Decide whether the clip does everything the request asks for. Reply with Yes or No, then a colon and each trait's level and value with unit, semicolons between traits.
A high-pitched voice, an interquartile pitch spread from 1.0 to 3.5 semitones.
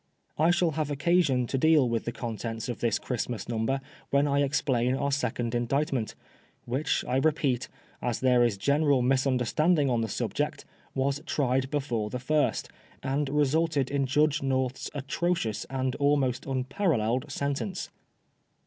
No: low, 135 Hz; average, 3.1 semitones